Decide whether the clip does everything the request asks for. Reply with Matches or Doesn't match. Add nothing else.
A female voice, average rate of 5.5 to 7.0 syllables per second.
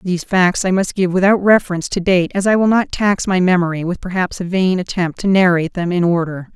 Matches